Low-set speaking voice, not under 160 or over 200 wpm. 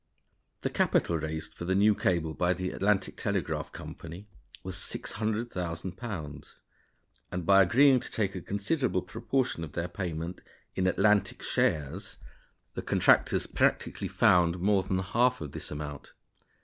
No: very low, 95 Hz; slow, 135 wpm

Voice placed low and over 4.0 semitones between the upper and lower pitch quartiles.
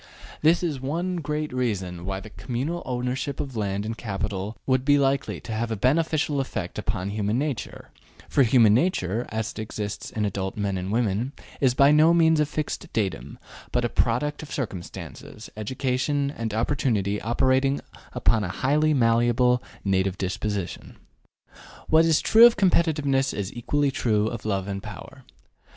Yes: low, 120 Hz; wide, 5.5 semitones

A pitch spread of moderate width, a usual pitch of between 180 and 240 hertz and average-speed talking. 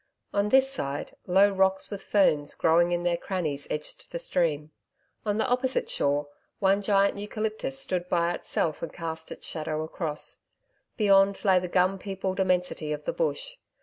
Yes: average, 4.0 semitones; medium, 185 Hz; average, 165 wpm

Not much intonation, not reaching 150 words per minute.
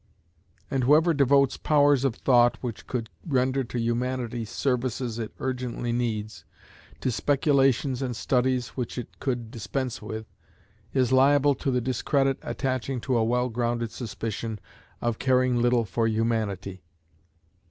Yes: narrow, 2.3 semitones; slow, 135 wpm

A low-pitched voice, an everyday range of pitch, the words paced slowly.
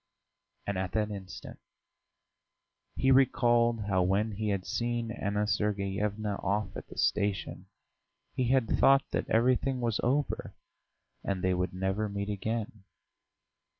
Yes: low, 105 Hz; average, 3.1 semitones; slow, 130 wpm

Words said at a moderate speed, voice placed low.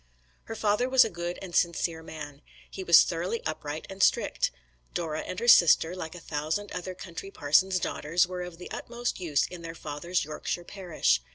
No: average, 185 wpm; medium, 175 Hz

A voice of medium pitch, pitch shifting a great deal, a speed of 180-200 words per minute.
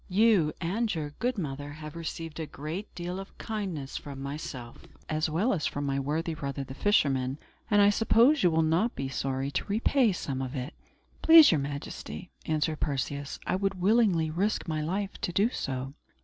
Yes: medium, 160 Hz; wide, 5.9 semitones; average, 185 wpm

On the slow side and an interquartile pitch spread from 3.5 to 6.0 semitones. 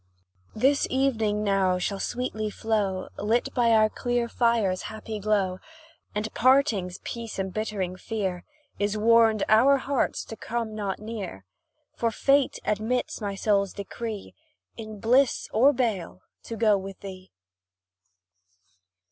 No: slow, 125 wpm; average, 2.8 semitones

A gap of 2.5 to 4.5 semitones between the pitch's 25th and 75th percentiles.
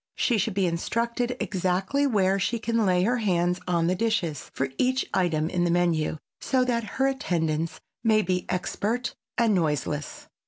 No: average, 5.2 semitones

